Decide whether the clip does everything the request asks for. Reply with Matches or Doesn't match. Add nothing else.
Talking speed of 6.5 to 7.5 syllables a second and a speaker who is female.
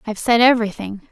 Matches